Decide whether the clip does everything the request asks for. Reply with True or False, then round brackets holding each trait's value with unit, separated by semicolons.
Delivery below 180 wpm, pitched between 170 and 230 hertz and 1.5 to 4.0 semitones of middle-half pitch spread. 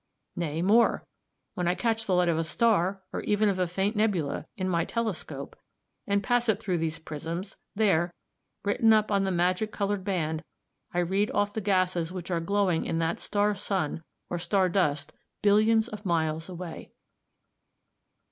True (170 wpm; 185 Hz; 3.4 semitones)